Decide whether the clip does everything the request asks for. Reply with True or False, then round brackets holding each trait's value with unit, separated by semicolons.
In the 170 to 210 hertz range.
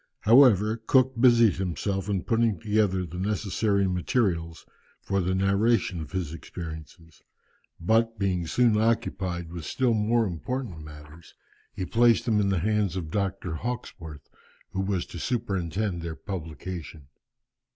False (95 Hz)